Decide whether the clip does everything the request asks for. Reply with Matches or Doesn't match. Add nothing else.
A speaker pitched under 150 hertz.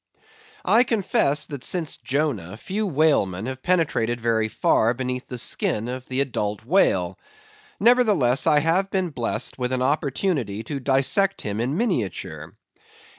Matches